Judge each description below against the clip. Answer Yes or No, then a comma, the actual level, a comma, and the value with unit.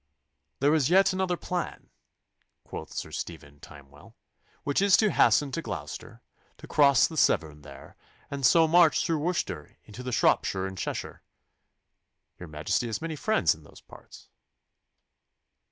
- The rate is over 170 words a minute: No, average, 140 wpm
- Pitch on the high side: No, medium, 140 Hz